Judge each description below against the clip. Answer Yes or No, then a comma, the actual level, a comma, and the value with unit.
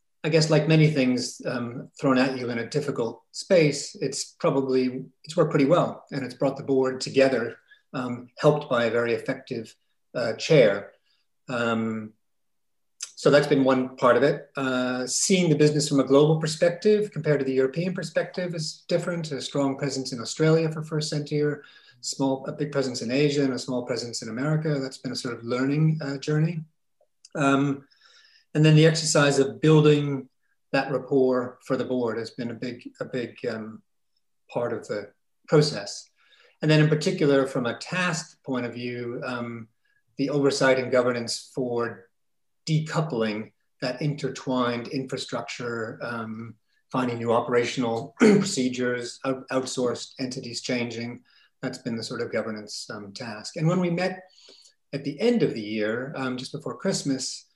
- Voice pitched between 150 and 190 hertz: No, low, 135 Hz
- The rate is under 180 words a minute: Yes, average, 165 wpm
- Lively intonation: No, average, 3.7 semitones